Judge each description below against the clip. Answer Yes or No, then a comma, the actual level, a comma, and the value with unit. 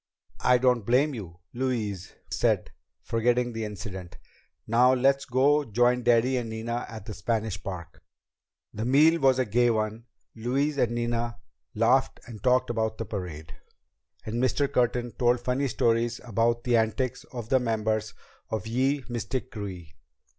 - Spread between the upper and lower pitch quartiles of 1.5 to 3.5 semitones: Yes, narrow, 2.5 semitones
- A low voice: Yes, low, 120 Hz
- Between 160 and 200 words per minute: No, average, 150 wpm